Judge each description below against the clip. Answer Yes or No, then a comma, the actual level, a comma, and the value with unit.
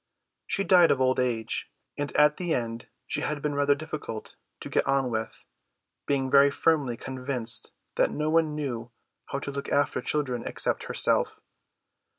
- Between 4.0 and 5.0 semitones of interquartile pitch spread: No, average, 3.1 semitones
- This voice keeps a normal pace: Yes, average, 165 wpm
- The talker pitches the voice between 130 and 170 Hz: Yes, medium, 140 Hz